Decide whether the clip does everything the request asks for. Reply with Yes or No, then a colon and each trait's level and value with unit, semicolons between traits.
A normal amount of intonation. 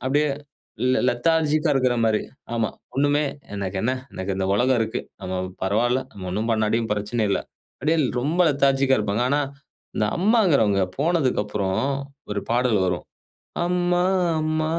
No: wide, 5.9 semitones